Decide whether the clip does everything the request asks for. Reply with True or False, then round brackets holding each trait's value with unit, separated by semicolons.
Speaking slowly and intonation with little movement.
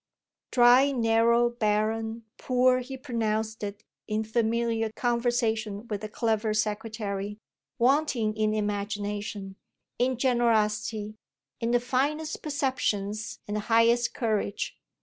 True (110 wpm; 2.2 semitones)